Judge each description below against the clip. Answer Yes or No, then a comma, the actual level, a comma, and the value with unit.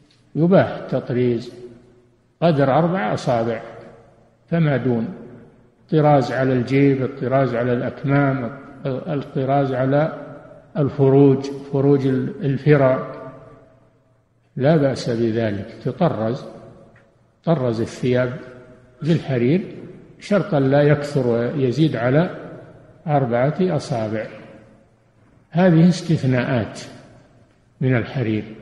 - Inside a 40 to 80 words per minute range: Yes, average, 75 wpm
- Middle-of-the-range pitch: No, low, 130 Hz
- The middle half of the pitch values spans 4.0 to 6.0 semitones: No, average, 3.4 semitones